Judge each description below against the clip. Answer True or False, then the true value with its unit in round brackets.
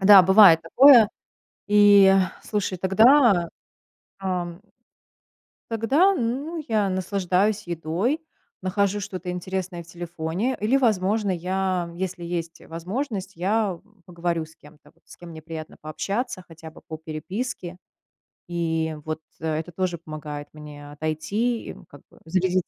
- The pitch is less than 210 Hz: True (185 Hz)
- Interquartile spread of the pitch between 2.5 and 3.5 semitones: False (4.0 semitones)